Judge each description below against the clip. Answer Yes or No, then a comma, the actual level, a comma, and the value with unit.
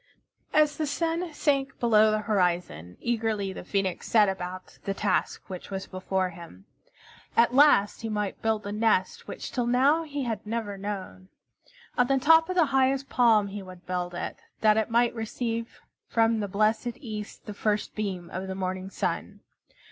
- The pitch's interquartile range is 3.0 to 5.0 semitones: Yes, average, 4.3 semitones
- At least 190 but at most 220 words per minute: No, average, 175 wpm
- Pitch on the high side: Yes, high, 215 Hz